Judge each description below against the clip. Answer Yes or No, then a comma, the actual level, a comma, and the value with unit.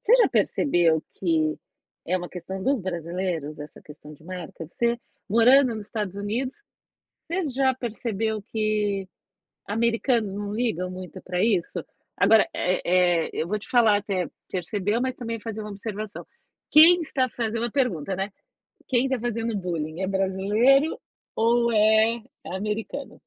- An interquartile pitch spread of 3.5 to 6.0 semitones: Yes, average, 4.2 semitones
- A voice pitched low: No, high, 210 Hz